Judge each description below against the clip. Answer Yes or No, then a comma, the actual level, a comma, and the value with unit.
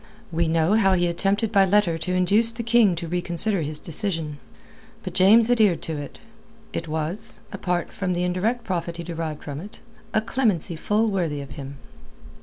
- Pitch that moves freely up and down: No, average, 4.2 semitones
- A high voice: No, medium, 180 Hz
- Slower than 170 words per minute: No, average, 180 wpm